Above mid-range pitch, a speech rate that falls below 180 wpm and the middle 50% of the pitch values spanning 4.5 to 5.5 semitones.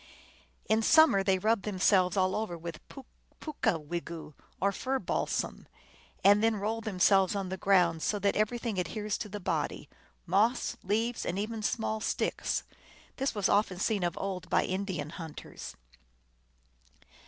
No: high, 200 Hz; average, 155 wpm; average, 3.1 semitones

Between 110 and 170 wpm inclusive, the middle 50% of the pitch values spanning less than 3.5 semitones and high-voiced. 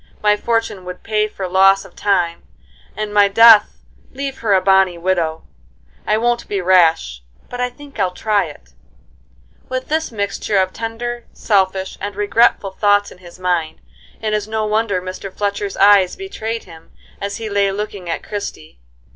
Yes: average, 165 wpm; average, 2.8 semitones; high, 200 Hz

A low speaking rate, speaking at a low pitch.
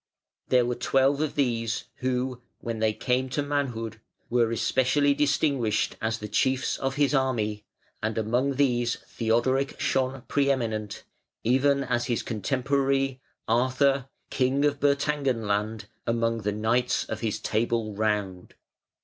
Yes: slow, 130 wpm; low, 125 Hz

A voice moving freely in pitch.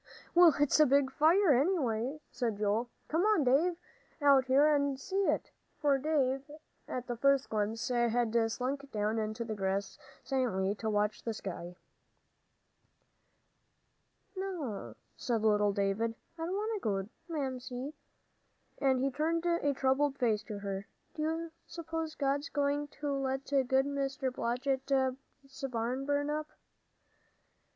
No: average, 4.3 semitones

